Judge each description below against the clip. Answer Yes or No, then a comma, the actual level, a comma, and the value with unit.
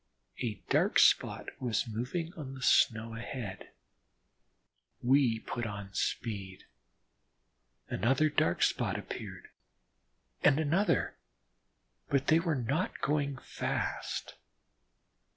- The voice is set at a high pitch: No, low, 125 Hz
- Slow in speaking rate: Yes, slow, 100 wpm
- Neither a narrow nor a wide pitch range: Yes, average, 4.5 semitones